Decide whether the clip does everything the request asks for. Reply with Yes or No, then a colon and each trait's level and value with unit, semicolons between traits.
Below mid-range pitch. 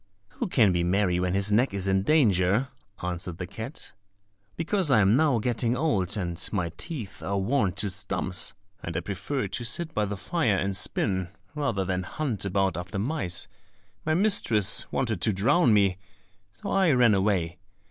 Yes: low, 100 Hz